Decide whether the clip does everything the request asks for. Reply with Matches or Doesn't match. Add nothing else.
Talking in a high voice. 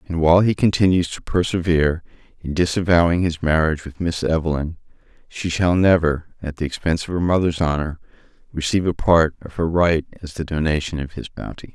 Doesn't match